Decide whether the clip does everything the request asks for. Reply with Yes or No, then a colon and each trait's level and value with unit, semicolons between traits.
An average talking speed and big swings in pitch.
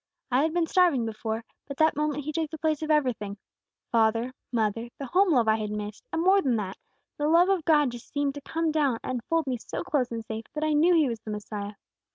No: fast, 235 wpm; wide, 5.7 semitones